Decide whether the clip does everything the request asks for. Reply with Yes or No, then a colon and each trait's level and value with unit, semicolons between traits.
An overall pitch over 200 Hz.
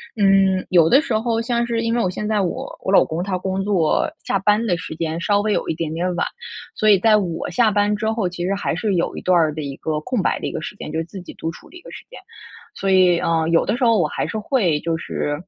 No: high, 190 Hz